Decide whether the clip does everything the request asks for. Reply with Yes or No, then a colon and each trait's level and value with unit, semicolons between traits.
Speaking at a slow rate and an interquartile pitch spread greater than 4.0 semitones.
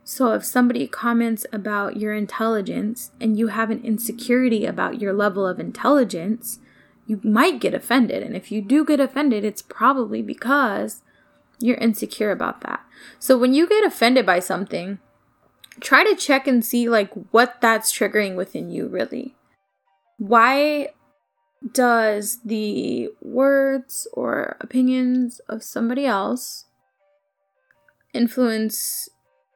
No: slow, 130 wpm; average, 3.4 semitones